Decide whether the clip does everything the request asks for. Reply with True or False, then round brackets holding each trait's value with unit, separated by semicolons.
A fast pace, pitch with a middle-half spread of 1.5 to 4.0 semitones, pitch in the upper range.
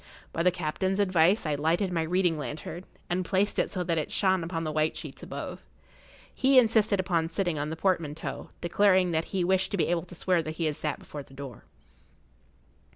False (210 wpm; 2.9 semitones; 175 Hz)